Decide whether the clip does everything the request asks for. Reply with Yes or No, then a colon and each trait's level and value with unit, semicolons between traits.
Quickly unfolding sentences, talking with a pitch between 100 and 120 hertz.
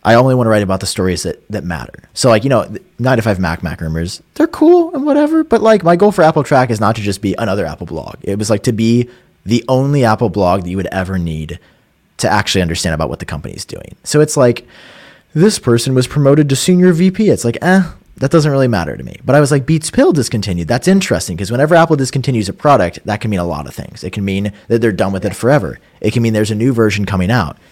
Yes: fast, 260 wpm; low, 115 Hz